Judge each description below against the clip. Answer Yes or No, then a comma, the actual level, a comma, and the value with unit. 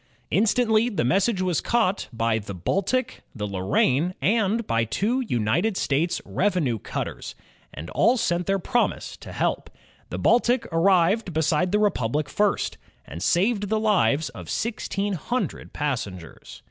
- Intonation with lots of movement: Yes, wide, 8.1 semitones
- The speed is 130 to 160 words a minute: Yes, average, 140 wpm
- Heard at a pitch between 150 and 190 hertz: Yes, medium, 185 Hz